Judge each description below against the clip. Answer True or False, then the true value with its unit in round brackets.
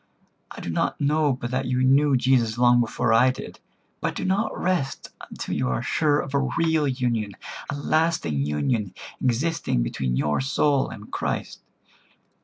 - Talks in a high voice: False (130 Hz)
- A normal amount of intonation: True (4.8 semitones)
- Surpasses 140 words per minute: True (160 wpm)